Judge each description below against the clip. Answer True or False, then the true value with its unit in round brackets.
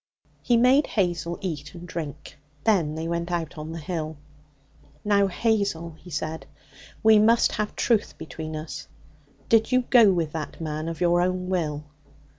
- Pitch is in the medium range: True (170 Hz)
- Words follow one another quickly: False (160 wpm)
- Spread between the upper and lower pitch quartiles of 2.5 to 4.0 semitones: False (4.4 semitones)